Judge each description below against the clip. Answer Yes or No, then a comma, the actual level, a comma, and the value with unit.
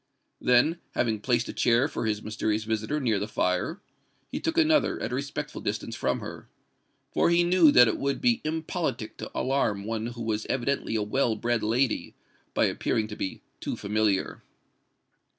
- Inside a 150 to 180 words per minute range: Yes, average, 170 wpm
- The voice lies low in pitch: Yes, low, 115 Hz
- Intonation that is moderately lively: Yes, average, 4.5 semitones